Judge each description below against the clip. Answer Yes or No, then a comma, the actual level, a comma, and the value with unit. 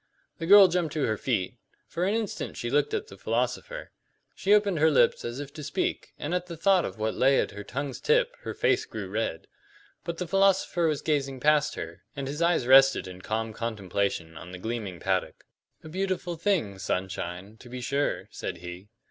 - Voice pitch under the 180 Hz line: Yes, medium, 140 Hz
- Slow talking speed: No, average, 200 wpm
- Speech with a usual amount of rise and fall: No, wide, 8.6 semitones